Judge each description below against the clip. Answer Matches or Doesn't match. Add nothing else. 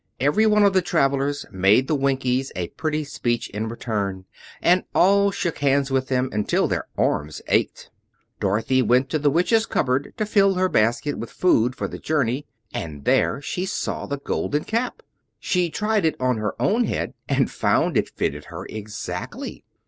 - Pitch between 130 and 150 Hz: Matches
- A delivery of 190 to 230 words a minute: Doesn't match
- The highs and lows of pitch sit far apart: Matches